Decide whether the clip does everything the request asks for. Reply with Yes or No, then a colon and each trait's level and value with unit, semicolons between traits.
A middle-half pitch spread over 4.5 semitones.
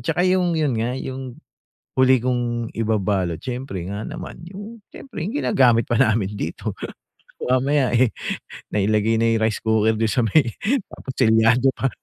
No: average, 3.3 semitones